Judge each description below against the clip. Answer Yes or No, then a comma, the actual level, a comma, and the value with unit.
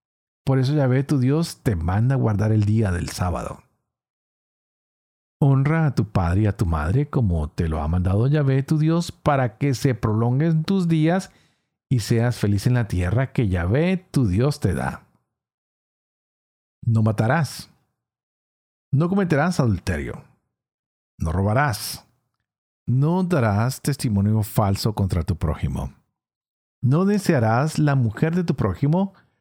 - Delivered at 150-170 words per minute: No, average, 140 wpm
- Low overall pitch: Yes, low, 120 Hz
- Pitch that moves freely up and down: Yes, wide, 6.8 semitones